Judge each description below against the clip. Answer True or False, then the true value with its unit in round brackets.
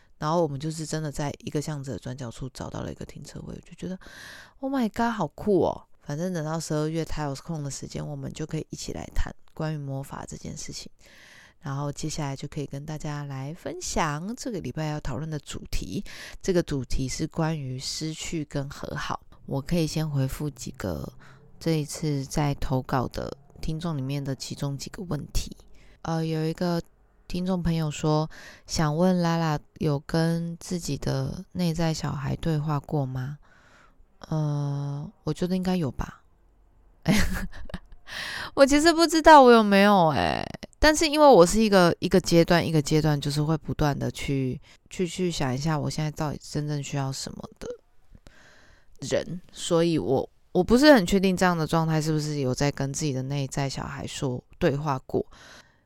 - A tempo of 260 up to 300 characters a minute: True (270 characters per minute)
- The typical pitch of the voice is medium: True (155 Hz)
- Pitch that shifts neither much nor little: True (3.3 semitones)